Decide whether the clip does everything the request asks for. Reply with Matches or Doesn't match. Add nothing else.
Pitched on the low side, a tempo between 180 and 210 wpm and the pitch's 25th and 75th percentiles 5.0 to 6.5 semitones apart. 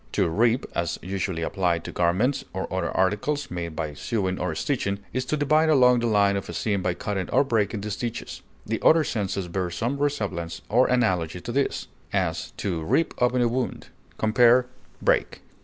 Matches